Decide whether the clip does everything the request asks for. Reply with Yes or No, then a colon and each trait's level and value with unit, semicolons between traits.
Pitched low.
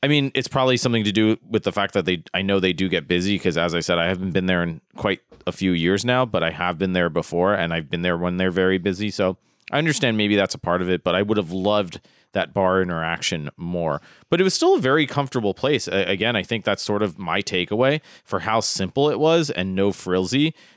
Yes: very low, 95 Hz